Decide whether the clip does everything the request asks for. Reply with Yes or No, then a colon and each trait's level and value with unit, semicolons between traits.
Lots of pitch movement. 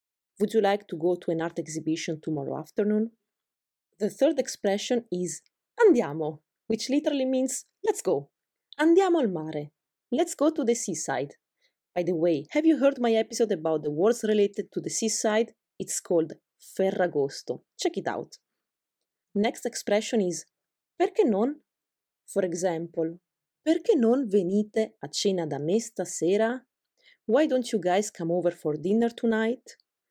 Yes: wide, 6.4 semitones